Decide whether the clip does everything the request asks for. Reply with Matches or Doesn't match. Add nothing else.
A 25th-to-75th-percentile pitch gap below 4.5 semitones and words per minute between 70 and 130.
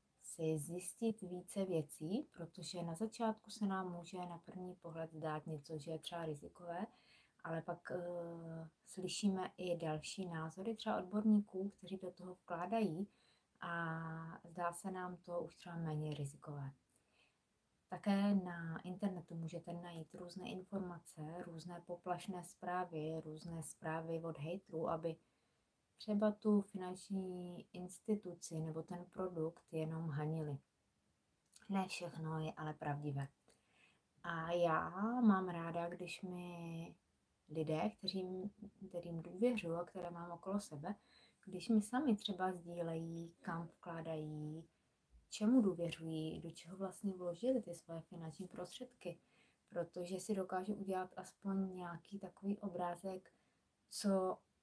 Matches